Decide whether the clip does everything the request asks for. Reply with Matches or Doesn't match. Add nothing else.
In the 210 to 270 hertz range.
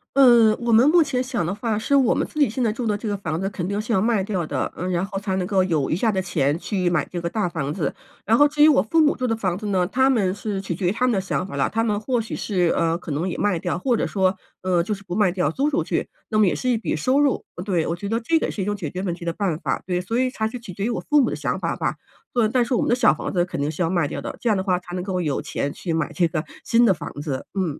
Doesn't match